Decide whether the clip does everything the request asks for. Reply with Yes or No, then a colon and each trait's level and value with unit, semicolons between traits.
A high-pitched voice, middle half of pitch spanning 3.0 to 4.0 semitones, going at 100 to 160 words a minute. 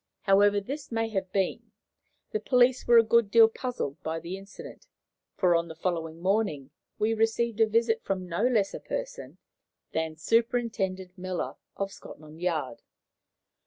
No: high, 195 Hz; average, 4.9 semitones; average, 155 wpm